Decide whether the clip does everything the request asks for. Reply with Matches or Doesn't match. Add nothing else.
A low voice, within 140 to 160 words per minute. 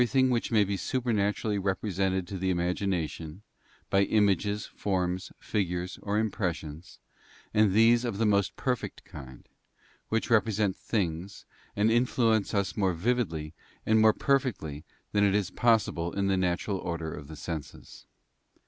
Matches